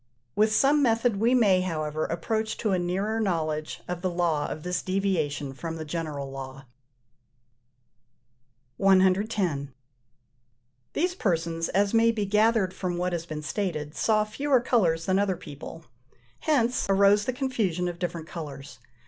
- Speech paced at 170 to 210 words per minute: No, average, 145 wpm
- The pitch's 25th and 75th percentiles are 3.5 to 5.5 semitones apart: Yes, average, 4.8 semitones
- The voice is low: No, medium, 185 Hz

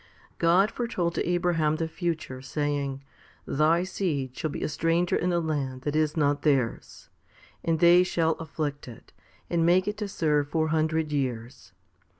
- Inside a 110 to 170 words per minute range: Yes, average, 165 wpm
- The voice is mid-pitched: Yes, medium, 155 Hz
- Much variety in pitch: No, average, 3.1 semitones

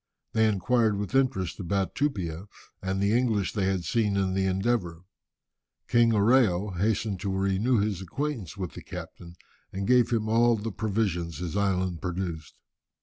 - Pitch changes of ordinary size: Yes, average, 3.4 semitones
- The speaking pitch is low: Yes, low, 100 Hz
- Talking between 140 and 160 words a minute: Yes, average, 155 wpm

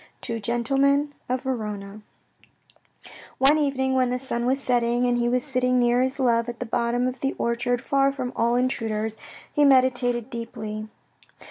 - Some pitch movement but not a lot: No, narrow, 2.0 semitones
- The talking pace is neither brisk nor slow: Yes, average, 160 wpm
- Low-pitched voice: No, high, 245 Hz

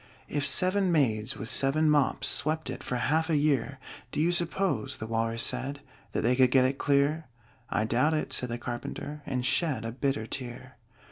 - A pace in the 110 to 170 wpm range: No, average, 190 wpm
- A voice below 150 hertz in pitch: Yes, low, 135 Hz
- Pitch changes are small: No, average, 4.0 semitones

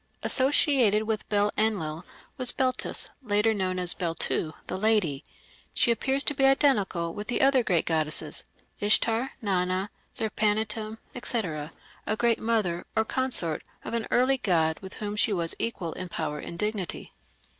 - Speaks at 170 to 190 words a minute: No, average, 150 wpm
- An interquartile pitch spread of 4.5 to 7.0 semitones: Yes, average, 4.8 semitones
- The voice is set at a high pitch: Yes, high, 210 Hz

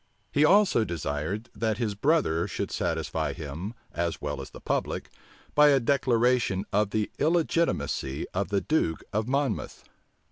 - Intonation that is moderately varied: No, wide, 7.1 semitones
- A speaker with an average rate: Yes, average, 145 wpm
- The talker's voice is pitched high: No, low, 110 Hz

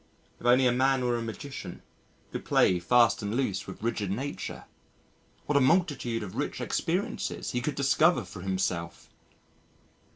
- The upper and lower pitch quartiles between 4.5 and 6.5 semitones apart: Yes, average, 5.0 semitones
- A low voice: Yes, low, 120 Hz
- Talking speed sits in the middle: Yes, average, 155 wpm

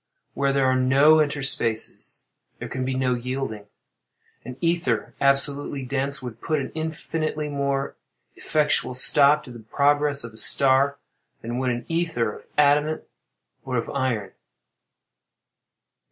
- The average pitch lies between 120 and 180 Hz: Yes, medium, 140 Hz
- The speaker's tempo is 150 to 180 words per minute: No, slow, 135 wpm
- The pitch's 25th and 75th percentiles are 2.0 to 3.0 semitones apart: Yes, narrow, 2.6 semitones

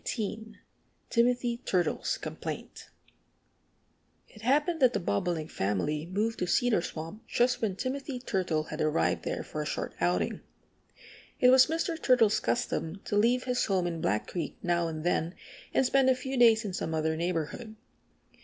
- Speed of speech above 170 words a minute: No, average, 160 wpm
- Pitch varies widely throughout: Yes, wide, 7.2 semitones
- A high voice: Yes, high, 210 Hz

